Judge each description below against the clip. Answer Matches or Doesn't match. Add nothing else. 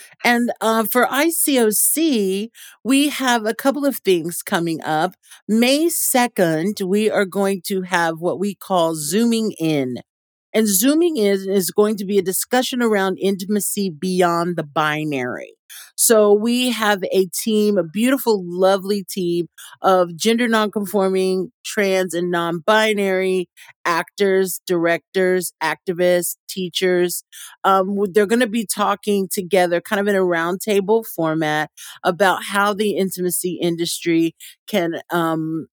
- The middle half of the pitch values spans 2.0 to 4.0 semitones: Matches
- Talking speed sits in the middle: Doesn't match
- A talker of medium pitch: Doesn't match